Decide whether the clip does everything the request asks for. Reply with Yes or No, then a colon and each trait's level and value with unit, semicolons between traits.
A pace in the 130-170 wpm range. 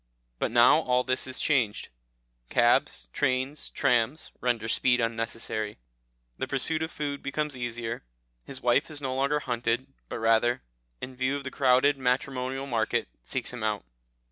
Yes: average, 150 wpm